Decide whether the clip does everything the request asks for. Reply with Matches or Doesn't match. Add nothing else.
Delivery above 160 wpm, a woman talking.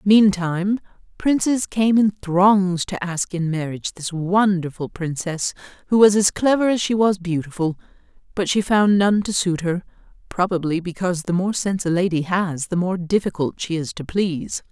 Matches